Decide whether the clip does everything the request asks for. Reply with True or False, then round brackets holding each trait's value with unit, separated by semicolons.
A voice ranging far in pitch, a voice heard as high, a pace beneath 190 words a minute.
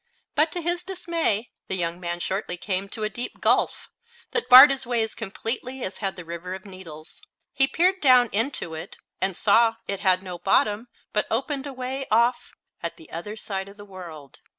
False (5.8 semitones; 210 Hz; 195 wpm)